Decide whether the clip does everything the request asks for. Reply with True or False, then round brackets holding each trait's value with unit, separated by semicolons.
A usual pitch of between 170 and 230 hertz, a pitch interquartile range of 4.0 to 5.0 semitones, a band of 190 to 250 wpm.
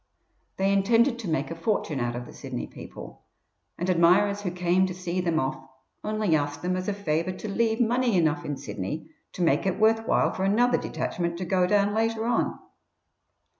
True (185 Hz; 4.3 semitones; 195 wpm)